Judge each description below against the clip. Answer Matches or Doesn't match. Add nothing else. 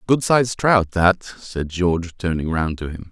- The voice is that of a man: Matches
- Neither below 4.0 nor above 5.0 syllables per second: Matches